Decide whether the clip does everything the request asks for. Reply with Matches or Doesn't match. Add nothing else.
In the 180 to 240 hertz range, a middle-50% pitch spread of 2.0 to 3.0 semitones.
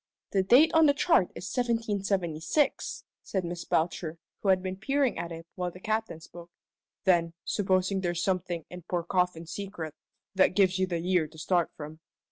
Matches